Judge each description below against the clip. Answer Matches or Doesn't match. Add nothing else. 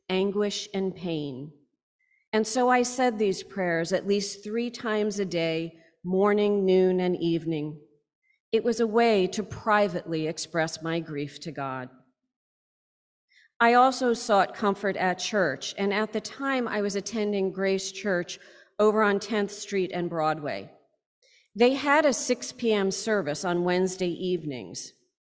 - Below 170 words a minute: Matches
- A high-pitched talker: Matches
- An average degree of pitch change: Matches